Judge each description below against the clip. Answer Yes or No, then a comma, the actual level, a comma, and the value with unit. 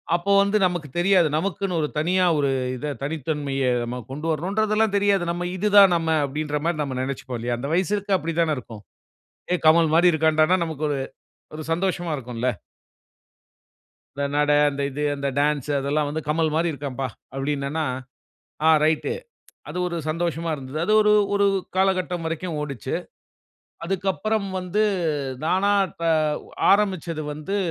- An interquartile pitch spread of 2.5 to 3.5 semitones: No, average, 4.2 semitones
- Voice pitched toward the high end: No, medium, 160 Hz